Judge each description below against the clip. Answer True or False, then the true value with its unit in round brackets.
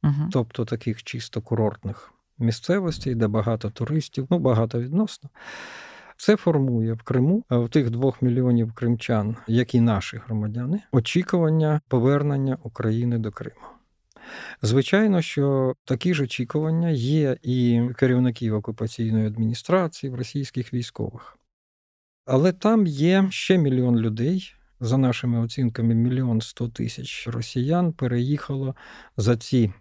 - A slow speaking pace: False (115 wpm)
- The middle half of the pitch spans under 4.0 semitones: False (4.3 semitones)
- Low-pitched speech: True (125 Hz)